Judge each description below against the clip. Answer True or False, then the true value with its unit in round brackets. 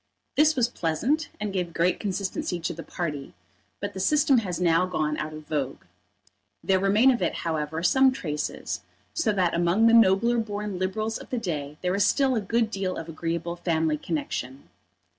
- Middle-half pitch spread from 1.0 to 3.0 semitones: False (5.1 semitones)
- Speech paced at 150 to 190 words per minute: True (180 wpm)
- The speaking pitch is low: False (185 Hz)